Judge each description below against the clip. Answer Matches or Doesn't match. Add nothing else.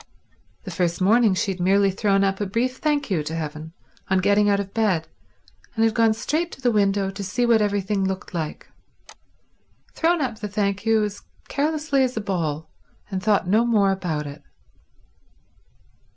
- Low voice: Doesn't match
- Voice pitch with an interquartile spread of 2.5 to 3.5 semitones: Matches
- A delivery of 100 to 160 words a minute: Doesn't match